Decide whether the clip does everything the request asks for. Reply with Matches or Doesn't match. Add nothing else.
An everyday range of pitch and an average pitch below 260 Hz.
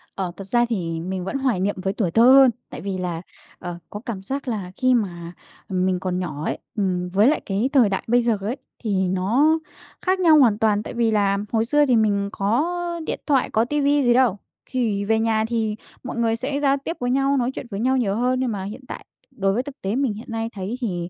Matches